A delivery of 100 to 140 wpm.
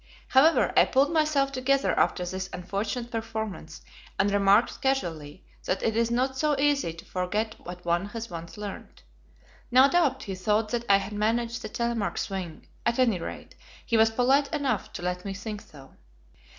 No: average, 175 wpm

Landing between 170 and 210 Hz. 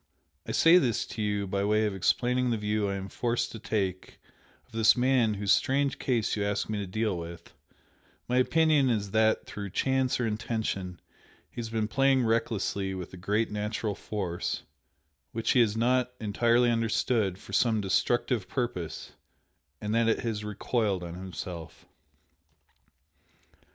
No: low, 110 Hz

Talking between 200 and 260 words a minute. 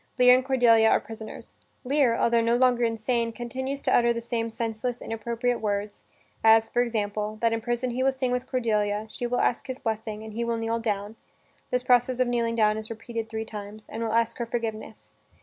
Yes: fast, 205 wpm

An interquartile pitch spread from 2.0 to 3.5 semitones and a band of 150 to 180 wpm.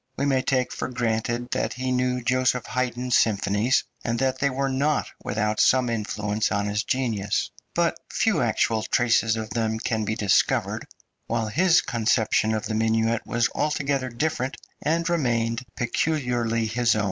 Yes: average, 2.7 semitones; average, 160 wpm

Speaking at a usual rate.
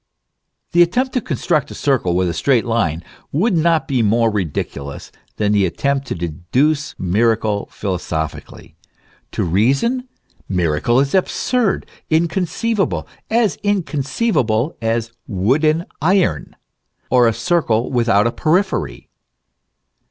No: slow, 115 wpm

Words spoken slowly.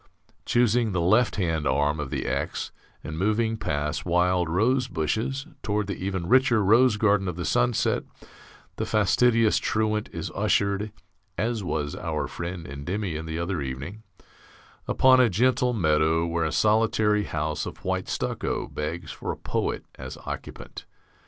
No: average, 150 wpm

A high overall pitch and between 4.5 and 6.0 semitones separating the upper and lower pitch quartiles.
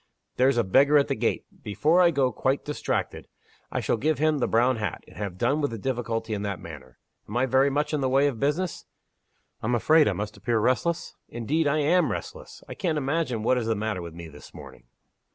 No: low, 130 Hz; average, 5.1 semitones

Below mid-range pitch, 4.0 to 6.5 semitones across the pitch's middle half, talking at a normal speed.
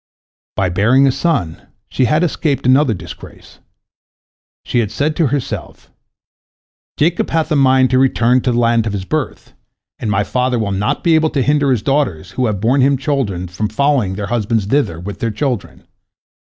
Yes: low, 125 Hz; average, 5.3 semitones; average, 180 wpm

